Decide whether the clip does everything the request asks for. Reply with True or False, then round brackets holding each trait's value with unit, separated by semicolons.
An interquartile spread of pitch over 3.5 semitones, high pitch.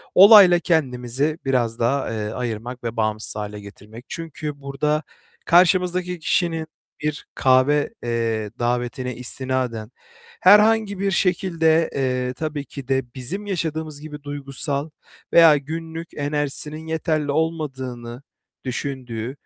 False (4.6 semitones; 145 Hz)